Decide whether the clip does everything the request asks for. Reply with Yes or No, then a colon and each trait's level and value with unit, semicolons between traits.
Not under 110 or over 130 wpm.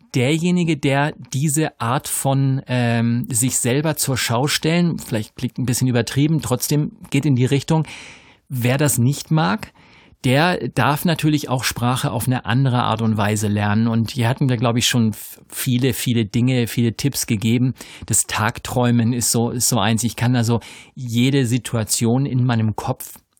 No: average, 165 wpm